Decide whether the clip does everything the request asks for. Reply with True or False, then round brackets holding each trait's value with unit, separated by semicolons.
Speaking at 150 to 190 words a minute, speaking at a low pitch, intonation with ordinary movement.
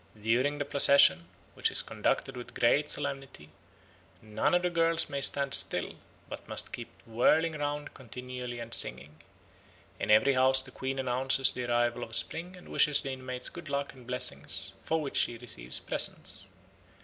True (165 wpm; 130 Hz; 3.2 semitones)